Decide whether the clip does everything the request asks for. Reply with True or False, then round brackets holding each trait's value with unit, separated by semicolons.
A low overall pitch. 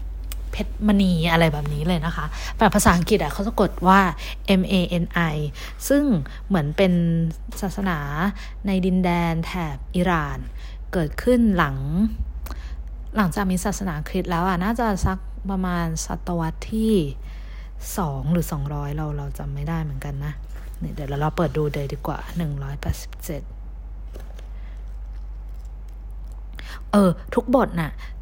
False (170 Hz)